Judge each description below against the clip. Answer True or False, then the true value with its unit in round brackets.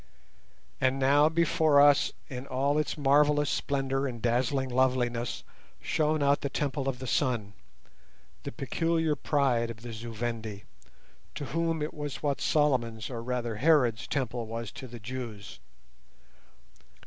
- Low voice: True (130 Hz)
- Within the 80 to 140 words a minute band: True (135 wpm)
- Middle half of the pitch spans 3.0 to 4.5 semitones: True (3.7 semitones)